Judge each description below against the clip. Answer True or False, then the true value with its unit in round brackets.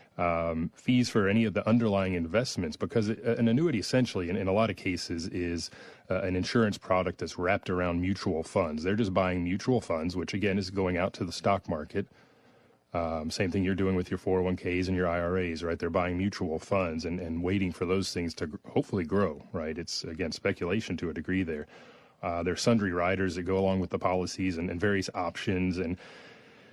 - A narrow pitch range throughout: True (2.2 semitones)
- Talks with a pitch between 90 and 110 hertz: True (95 Hz)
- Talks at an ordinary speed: False (215 wpm)